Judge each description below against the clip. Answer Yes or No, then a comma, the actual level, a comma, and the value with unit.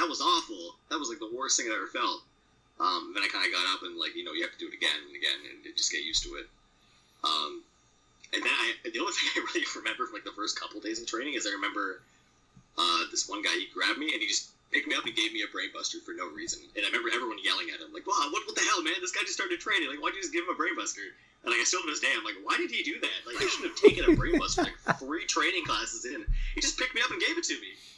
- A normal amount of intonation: No, narrow, 2.1 semitones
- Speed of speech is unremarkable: No, fast, 305 wpm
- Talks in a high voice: Yes, very high, 340 Hz